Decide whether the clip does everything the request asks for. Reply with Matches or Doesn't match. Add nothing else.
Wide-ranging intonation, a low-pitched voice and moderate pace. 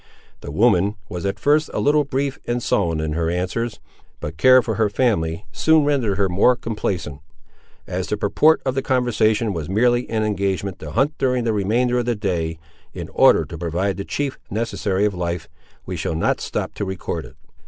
Matches